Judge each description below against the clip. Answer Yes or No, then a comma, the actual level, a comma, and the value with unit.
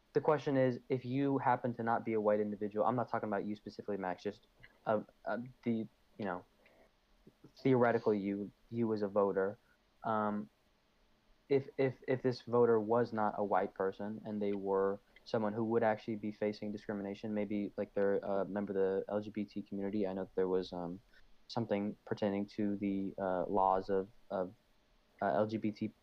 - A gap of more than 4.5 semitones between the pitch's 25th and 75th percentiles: No, narrow, 2.6 semitones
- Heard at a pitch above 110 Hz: No, low, 105 Hz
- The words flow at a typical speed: Yes, average, 180 wpm